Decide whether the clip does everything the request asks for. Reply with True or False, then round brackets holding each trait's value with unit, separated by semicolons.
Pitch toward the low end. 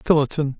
False (145 Hz)